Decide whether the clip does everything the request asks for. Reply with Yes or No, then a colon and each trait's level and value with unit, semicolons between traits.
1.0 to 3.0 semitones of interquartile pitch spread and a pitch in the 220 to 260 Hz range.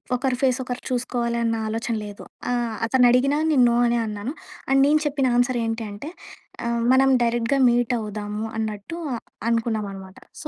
Yes: average, 2.7 semitones; high, 235 Hz